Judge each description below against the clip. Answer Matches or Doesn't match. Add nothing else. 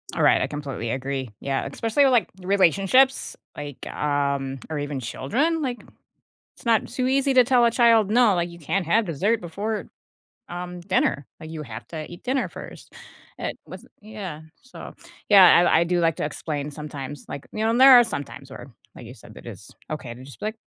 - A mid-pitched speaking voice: Matches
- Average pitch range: Doesn't match